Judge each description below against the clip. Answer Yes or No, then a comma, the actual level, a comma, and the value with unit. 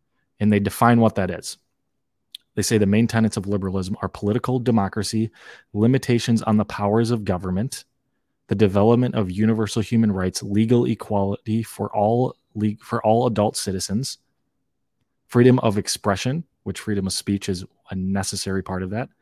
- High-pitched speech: No, low, 105 Hz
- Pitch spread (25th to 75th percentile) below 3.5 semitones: Yes, narrow, 2.4 semitones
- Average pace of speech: Yes, average, 155 wpm